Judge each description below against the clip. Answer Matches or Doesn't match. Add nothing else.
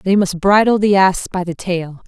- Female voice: Matches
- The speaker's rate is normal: Doesn't match